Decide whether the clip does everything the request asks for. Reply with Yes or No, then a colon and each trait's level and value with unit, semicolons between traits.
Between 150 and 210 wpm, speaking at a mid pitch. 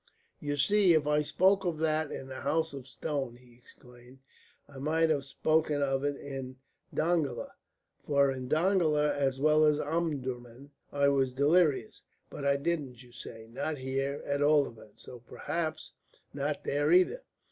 Yes: average, 165 wpm; medium, 145 Hz